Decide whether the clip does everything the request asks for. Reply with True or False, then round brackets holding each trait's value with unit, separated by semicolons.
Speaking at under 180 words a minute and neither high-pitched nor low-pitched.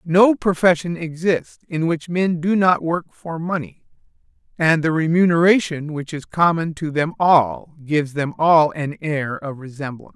True (160 wpm; 160 Hz)